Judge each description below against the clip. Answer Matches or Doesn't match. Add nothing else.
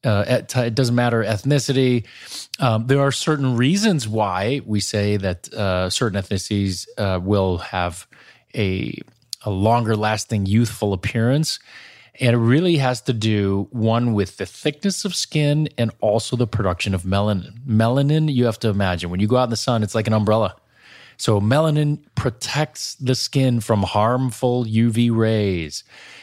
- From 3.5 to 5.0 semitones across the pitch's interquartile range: Matches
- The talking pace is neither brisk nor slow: Matches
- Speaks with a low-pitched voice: Matches